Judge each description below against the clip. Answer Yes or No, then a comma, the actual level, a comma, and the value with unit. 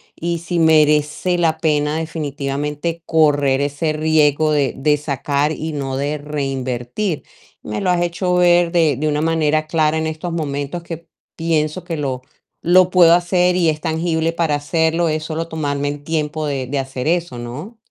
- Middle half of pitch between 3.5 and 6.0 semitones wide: No, narrow, 2.5 semitones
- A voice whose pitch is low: No, medium, 155 Hz